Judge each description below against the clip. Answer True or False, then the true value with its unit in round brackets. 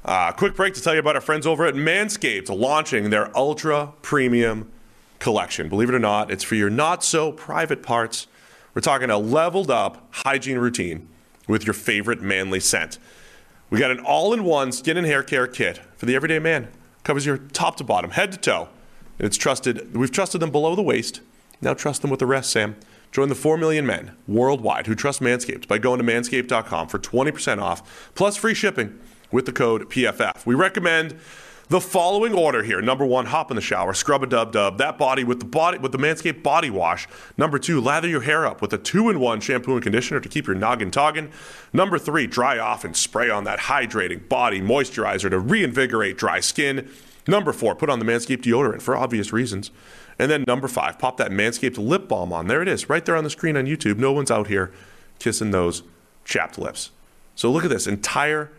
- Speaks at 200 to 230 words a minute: True (205 wpm)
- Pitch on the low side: True (130 Hz)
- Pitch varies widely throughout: True (5.9 semitones)